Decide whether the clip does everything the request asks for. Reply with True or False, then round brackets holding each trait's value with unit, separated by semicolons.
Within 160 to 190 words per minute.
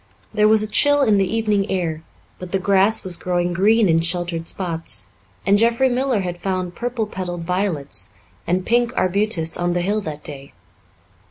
True (175 wpm)